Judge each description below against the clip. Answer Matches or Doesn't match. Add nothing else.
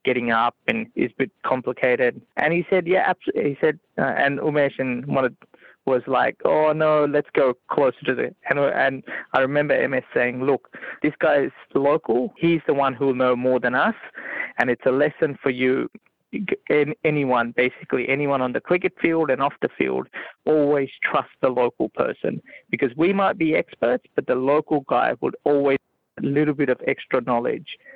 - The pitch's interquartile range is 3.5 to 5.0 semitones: Matches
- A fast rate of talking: Matches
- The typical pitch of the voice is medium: Matches